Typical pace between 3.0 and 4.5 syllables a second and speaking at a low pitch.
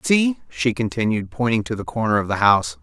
No: 5.6 syllables/s; low, 115 Hz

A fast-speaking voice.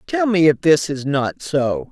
Yes: fast, 220 wpm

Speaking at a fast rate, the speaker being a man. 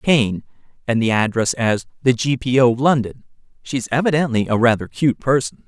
No: average, 170 wpm; male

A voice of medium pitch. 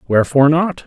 Yes: medium, 150 Hz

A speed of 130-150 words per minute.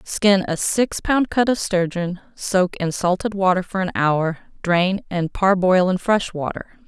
No: average, 175 wpm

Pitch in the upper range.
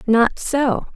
Yes: very high, 250 Hz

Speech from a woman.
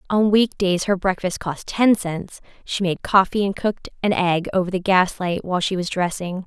Yes: female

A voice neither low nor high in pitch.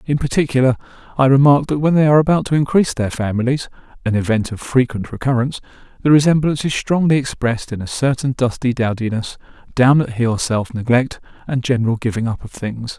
No: low, 130 Hz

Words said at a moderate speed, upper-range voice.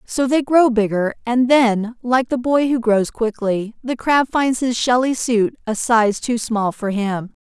Yes: average, 195 wpm; high, 235 Hz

